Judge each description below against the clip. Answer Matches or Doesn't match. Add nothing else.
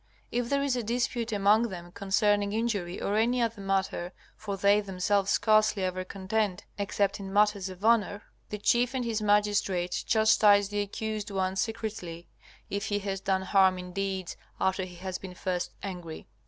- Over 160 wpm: Matches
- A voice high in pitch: Matches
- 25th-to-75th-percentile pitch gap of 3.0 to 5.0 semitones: Doesn't match